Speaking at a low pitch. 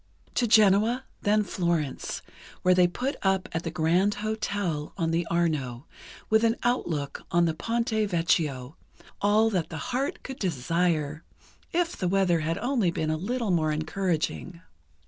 No: medium, 180 Hz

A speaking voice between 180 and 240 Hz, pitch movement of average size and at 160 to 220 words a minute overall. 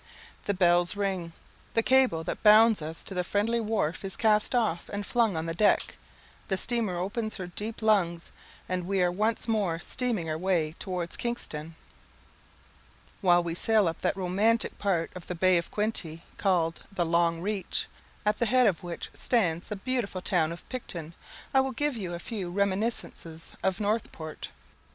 Yes: high, 190 Hz; average, 4.1 semitones; average, 175 wpm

